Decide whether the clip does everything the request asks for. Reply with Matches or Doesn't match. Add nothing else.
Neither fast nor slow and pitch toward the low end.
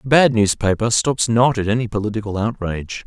Matches